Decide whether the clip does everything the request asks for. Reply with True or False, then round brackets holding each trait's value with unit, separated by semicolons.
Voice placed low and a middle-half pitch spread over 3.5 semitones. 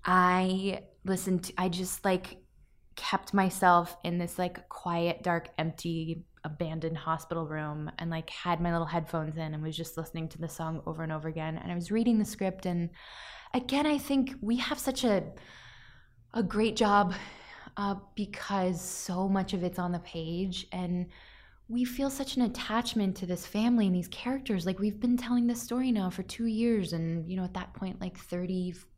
False (185 Hz; 3.9 semitones)